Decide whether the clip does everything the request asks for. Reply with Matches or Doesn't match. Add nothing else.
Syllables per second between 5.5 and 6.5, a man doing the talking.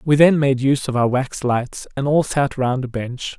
Doesn't match